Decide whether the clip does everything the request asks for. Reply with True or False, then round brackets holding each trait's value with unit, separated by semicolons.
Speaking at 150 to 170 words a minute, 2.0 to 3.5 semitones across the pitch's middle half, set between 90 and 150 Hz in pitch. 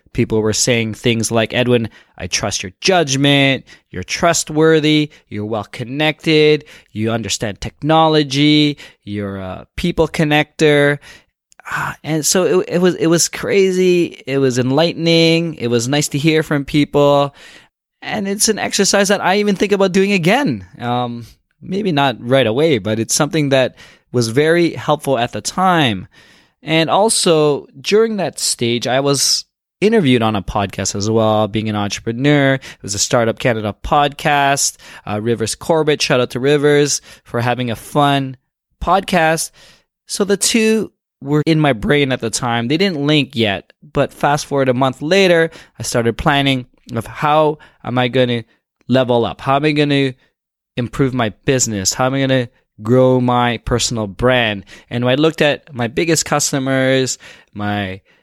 False (160 wpm; 5.0 semitones; 135 Hz)